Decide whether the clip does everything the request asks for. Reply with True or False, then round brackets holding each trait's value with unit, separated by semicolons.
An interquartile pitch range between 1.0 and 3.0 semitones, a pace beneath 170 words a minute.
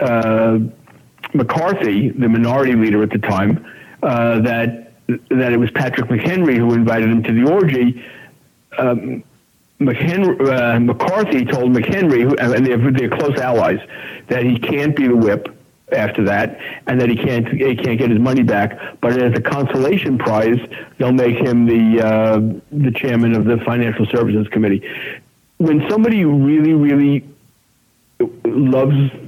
True (2.7 semitones; 145 wpm)